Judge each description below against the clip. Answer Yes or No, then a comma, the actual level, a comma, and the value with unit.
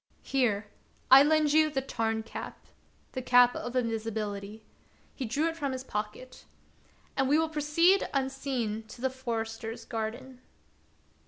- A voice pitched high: Yes, very high, 255 Hz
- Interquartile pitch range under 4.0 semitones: Yes, average, 3.6 semitones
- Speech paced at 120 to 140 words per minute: No, average, 155 wpm